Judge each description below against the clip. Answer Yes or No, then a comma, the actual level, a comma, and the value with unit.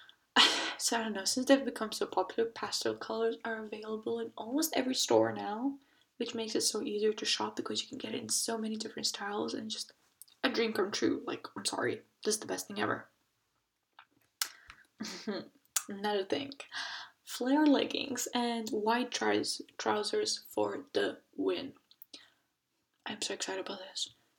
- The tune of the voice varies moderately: Yes, average, 3.0 semitones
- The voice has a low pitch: No, high, 230 Hz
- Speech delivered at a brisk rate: No, average, 160 wpm